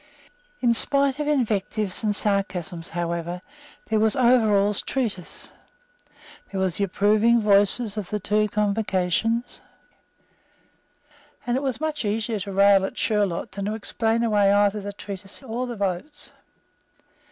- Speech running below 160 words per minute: Yes, slow, 135 wpm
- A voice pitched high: Yes, high, 210 Hz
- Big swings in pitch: No, average, 2.8 semitones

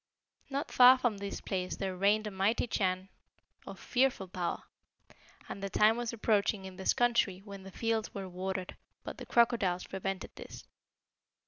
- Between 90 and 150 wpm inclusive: No, average, 160 wpm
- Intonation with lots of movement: No, average, 3.2 semitones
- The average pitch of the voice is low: No, high, 200 Hz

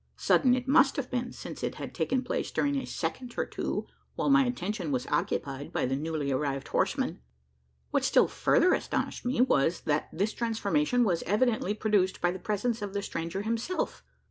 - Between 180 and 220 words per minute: Yes, average, 185 wpm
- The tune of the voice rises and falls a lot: Yes, wide, 7.1 semitones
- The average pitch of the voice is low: No, high, 210 Hz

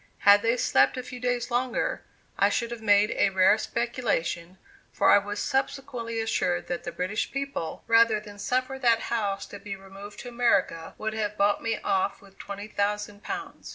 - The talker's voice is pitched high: Yes, high, 215 Hz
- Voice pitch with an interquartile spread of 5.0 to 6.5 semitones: No, average, 3.1 semitones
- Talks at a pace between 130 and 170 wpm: No, average, 185 wpm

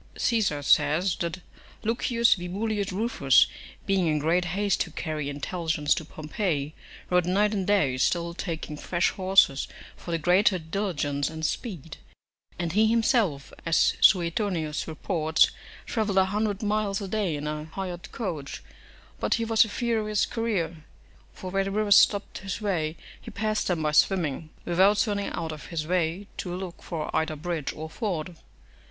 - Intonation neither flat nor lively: Yes, average, 4.4 semitones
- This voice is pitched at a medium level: Yes, medium, 180 Hz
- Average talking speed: Yes, average, 160 wpm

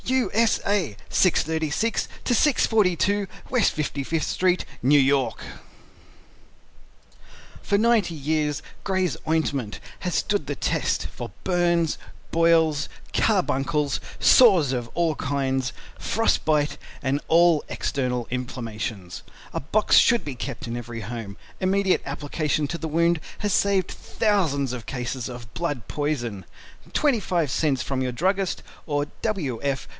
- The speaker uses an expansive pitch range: Yes, wide, 5.7 semitones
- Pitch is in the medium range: Yes, medium, 150 Hz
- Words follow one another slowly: Yes, slow, 125 wpm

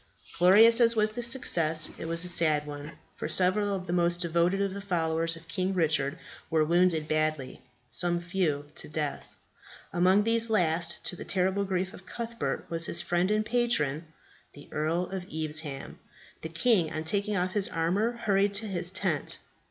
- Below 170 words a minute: No, average, 175 wpm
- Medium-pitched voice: Yes, medium, 175 Hz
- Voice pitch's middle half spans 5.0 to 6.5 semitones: No, average, 3.7 semitones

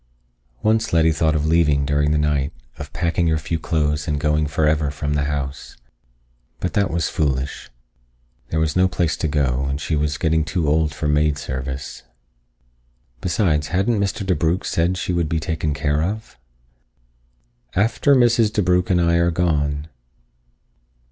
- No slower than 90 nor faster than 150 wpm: No, average, 160 wpm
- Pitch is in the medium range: No, very low, 80 Hz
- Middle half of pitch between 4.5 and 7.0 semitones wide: No, average, 2.9 semitones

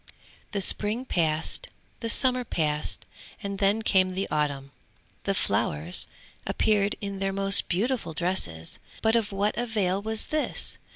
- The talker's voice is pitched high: Yes, high, 195 Hz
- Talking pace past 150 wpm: No, slow, 135 wpm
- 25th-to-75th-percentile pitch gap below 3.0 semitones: No, average, 4.4 semitones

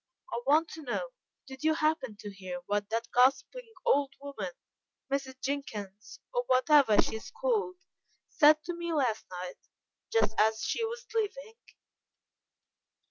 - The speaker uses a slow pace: No, average, 145 wpm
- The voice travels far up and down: Yes, wide, 8.0 semitones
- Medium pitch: No, very high, 280 Hz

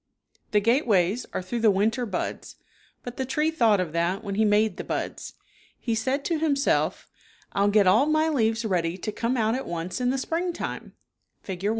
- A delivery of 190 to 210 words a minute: Yes, average, 195 wpm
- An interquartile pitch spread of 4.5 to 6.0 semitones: Yes, average, 4.9 semitones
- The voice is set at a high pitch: Yes, high, 225 Hz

